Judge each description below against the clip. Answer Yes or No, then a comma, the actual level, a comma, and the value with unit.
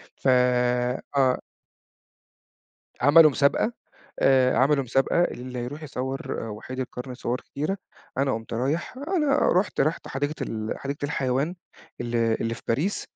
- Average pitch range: Yes, average, 3.2 semitones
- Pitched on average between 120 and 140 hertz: Yes, low, 135 Hz